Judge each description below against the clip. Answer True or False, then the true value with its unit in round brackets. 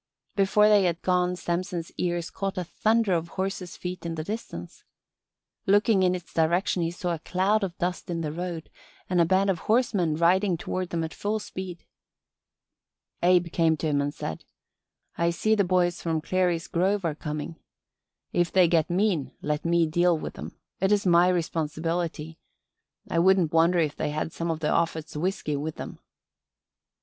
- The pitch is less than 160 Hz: False (175 Hz)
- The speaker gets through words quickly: False (175 wpm)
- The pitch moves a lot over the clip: False (2.4 semitones)